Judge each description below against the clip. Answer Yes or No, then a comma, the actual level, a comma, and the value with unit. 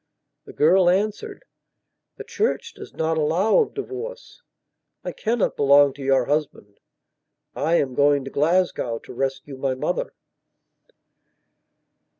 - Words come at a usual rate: No, slow, 125 wpm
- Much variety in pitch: Yes, wide, 7.6 semitones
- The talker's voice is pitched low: No, medium, 155 Hz